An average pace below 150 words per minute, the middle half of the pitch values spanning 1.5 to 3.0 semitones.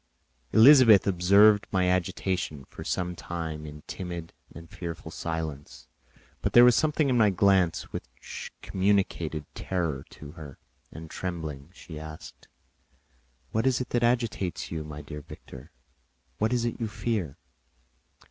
No: average, 140 wpm; wide, 5.6 semitones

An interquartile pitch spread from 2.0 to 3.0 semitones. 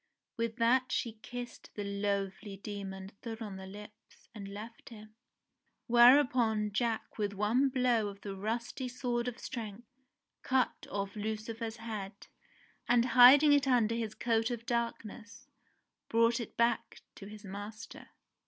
Yes: narrow, 2.6 semitones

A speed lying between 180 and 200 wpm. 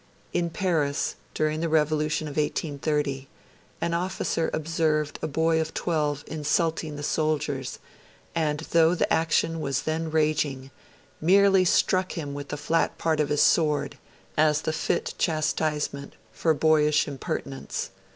No: slow, 135 wpm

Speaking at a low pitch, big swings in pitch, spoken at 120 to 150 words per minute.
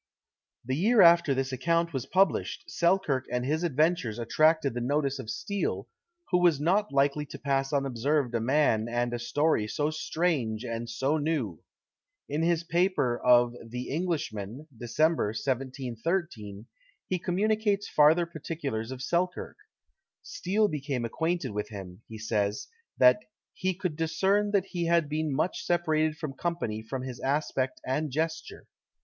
No: medium, 145 Hz; wide, 5.7 semitones; average, 145 wpm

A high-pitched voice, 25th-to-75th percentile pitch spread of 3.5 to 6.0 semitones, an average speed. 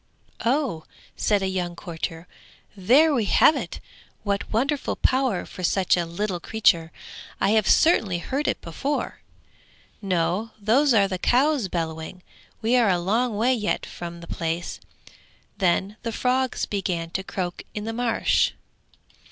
Yes: high, 200 Hz; wide, 5.6 semitones; average, 145 wpm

